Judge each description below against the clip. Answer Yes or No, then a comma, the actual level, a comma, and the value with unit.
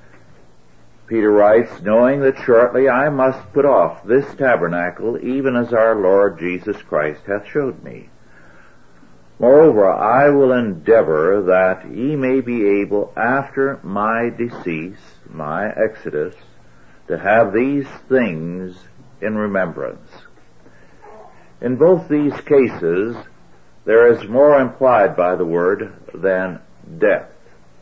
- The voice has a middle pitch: No, low, 115 Hz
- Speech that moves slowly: Yes, slow, 115 wpm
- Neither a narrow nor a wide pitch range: No, wide, 6.3 semitones